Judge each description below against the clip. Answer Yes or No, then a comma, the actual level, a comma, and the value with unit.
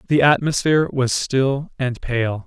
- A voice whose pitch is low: Yes, low, 130 Hz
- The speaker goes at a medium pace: Yes, average, 145 wpm